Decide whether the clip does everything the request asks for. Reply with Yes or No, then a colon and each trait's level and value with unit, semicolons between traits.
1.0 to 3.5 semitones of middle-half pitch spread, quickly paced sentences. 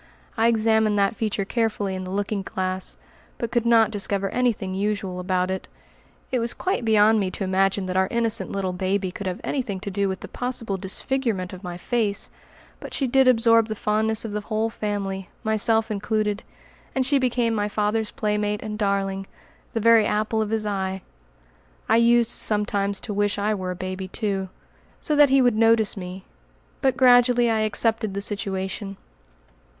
No: average, 2.7 semitones; average, 180 wpm